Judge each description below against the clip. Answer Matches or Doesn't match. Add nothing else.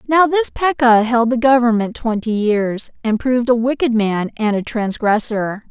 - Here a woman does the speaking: Matches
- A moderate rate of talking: Matches